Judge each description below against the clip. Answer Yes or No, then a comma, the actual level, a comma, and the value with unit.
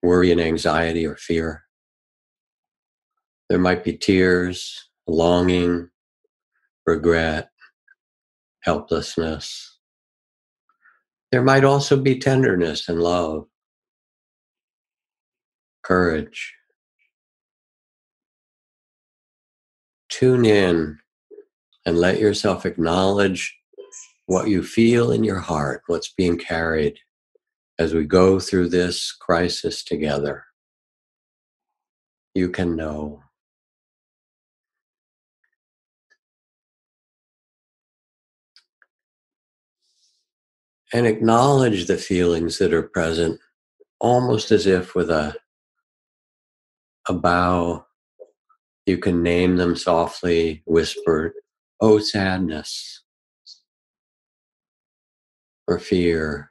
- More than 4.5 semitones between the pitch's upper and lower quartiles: Yes, average, 4.9 semitones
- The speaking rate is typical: No, slow, 75 wpm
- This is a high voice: No, very low, 90 Hz